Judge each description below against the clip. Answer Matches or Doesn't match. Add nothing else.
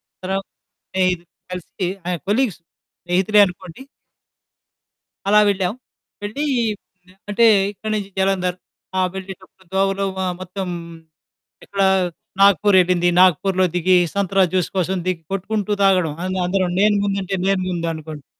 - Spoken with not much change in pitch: Matches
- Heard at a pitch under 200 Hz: Matches